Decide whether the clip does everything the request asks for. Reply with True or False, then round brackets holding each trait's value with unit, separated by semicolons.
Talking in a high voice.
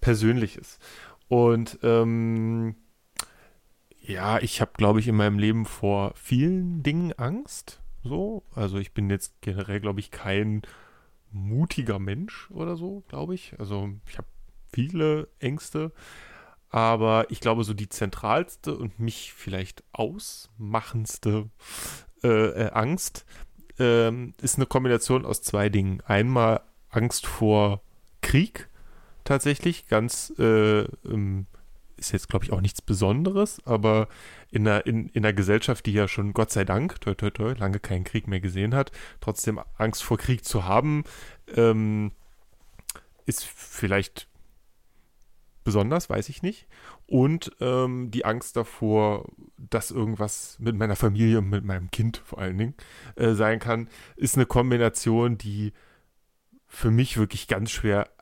False (110 Hz)